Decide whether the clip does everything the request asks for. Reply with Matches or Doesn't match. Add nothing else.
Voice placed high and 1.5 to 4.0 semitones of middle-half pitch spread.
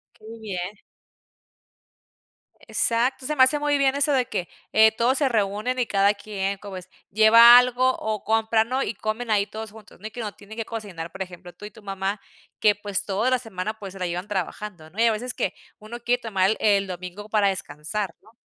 Matches